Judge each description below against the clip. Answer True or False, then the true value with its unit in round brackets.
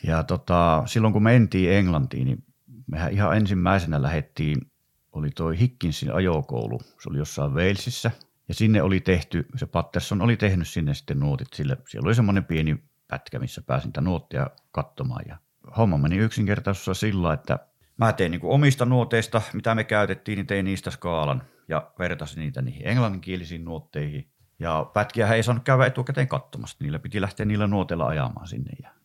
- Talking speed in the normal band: False (165 wpm)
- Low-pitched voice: True (100 Hz)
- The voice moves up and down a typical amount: False (5.7 semitones)